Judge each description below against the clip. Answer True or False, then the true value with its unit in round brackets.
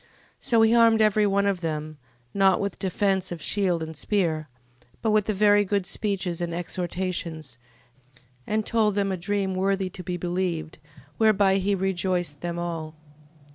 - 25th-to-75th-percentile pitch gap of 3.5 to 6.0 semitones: False (2.8 semitones)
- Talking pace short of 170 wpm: True (160 wpm)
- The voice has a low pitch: False (190 Hz)